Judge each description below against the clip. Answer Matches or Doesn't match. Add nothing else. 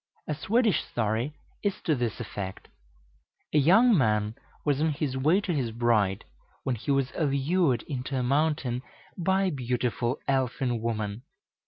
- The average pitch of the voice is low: Matches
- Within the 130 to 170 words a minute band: Matches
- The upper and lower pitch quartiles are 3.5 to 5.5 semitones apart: Matches